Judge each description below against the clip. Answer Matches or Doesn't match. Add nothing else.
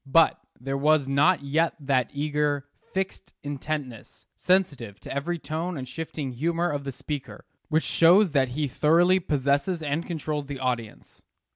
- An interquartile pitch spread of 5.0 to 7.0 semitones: Doesn't match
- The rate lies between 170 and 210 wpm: Doesn't match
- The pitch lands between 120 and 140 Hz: Doesn't match